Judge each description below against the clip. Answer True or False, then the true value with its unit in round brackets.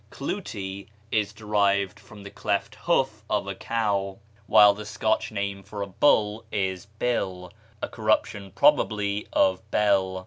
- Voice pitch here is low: True (100 Hz)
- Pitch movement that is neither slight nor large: False (1.5 semitones)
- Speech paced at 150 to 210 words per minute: False (140 wpm)